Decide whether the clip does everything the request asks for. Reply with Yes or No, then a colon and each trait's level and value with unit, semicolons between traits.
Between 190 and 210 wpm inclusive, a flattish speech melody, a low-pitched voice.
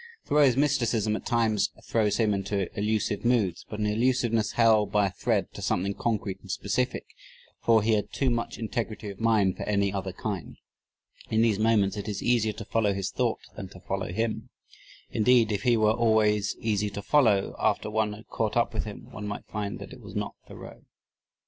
Yes: average, 195 wpm; narrow, 2.1 semitones; low, 110 Hz